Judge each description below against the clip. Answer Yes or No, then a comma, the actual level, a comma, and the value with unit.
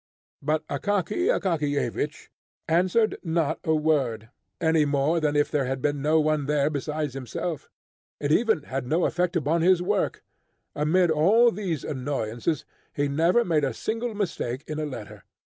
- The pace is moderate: Yes, average, 155 wpm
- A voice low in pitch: No, medium, 155 Hz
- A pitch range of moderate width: Yes, average, 3.5 semitones